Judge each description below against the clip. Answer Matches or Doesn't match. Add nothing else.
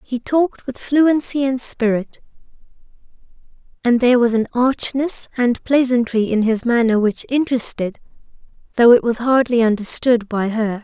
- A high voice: Matches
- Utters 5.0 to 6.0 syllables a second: Doesn't match